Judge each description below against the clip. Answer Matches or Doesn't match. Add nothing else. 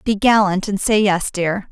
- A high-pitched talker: Matches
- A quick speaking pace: Matches